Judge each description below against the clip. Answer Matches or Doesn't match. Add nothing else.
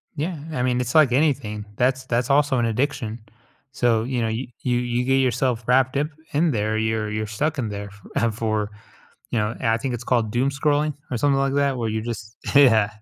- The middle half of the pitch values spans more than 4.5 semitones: Doesn't match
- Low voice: Matches